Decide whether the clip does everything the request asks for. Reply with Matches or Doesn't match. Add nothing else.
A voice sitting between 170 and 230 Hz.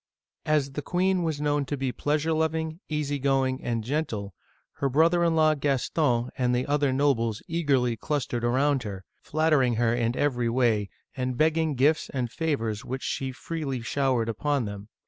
Doesn't match